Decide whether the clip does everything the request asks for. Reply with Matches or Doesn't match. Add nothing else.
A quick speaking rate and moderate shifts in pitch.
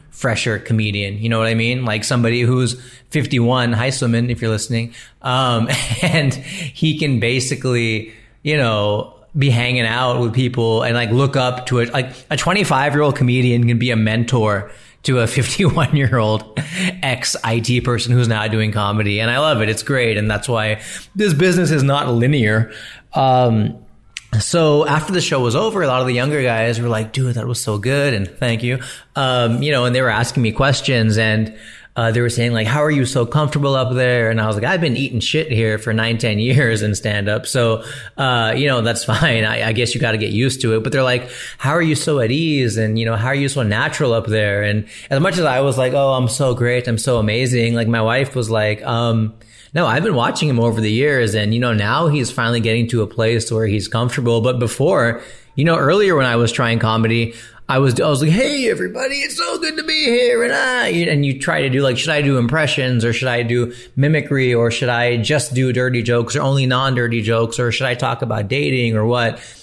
Matches